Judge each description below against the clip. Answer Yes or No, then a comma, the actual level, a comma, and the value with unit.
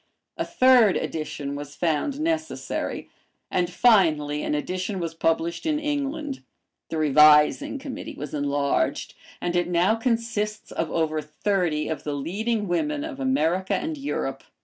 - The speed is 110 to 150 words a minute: Yes, average, 140 wpm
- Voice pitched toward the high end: No, medium, 180 Hz